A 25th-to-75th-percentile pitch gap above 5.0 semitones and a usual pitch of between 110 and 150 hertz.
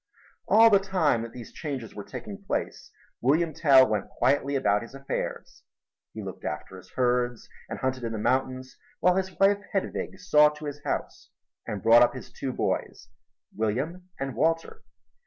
Yes: wide, 5.4 semitones; low, 135 Hz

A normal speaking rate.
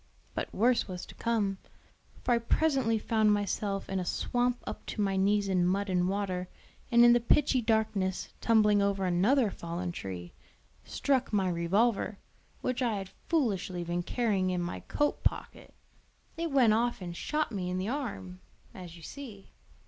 Yes: average, 170 wpm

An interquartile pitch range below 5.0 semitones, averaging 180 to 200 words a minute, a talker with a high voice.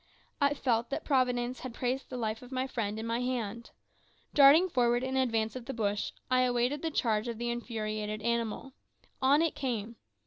Yes: narrow, 2.5 semitones; average, 185 wpm; high, 240 Hz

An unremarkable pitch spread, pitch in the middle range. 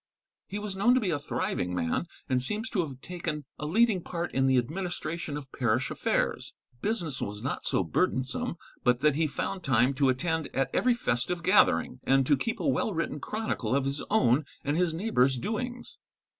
No: wide, 6.7 semitones; medium, 155 Hz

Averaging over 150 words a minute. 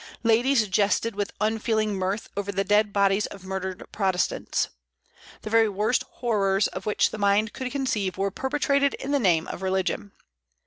Yes: average, 165 wpm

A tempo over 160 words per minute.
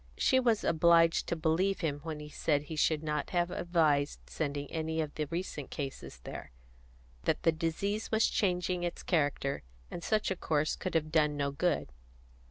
Yes: average, 180 wpm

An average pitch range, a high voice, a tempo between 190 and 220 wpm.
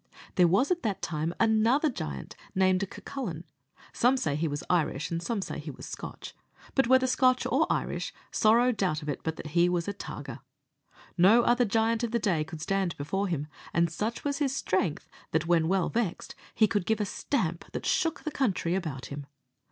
No: wide, 6.1 semitones; high, 195 Hz; average, 195 wpm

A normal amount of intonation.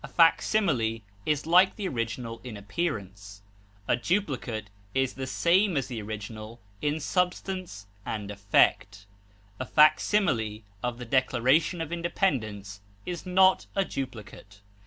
No: wide, 7.9 semitones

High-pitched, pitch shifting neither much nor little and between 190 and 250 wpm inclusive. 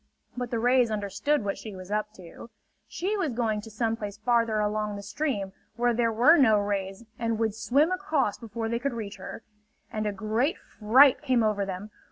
Yes: high, 225 Hz; average, 3.0 semitones; average, 200 wpm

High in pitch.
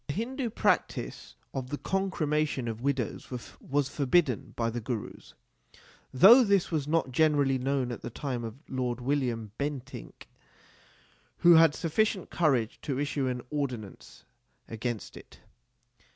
No: medium, 140 Hz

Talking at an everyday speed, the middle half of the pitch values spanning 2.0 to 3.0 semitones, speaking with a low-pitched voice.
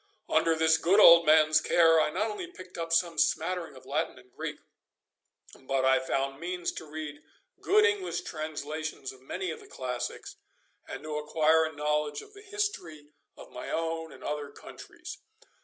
No: average, 175 wpm; narrow, 2.4 semitones; medium, 160 Hz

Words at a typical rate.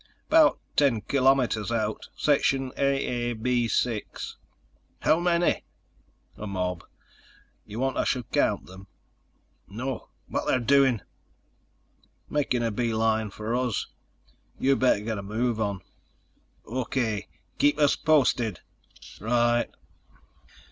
No: slow, 105 wpm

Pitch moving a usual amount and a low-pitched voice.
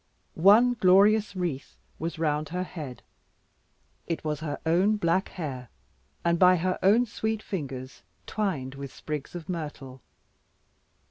No: average, 4.7 semitones; medium, 170 Hz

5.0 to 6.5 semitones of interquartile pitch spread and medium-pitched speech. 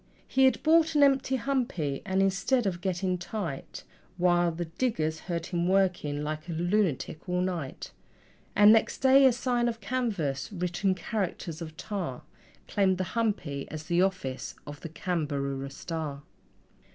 Yes: average, 5.3 semitones; medium, 180 Hz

